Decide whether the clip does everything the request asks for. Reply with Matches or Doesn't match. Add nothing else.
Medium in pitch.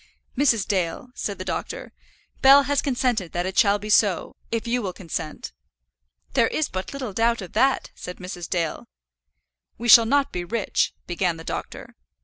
Doesn't match